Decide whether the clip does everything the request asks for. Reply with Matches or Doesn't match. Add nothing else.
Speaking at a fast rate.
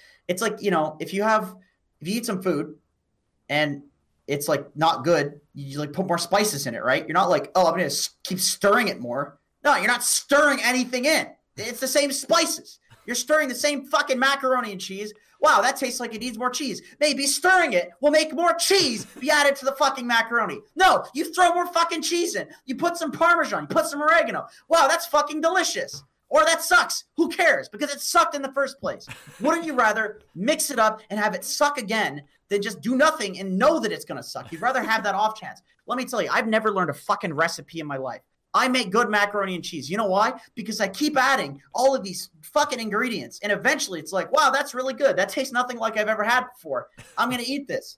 Matches